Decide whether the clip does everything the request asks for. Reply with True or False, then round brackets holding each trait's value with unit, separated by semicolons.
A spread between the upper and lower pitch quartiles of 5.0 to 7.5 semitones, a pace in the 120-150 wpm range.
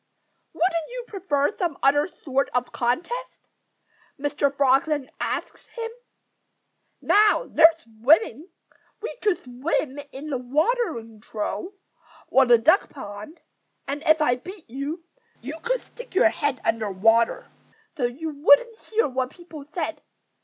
True (5.6 semitones; 135 wpm)